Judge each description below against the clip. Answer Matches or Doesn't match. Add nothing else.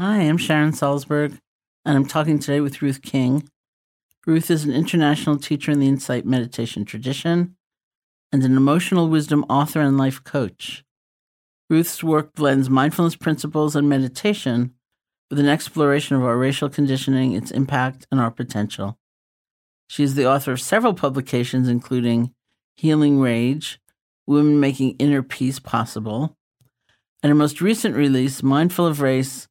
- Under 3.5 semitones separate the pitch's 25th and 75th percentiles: Matches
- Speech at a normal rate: Matches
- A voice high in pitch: Doesn't match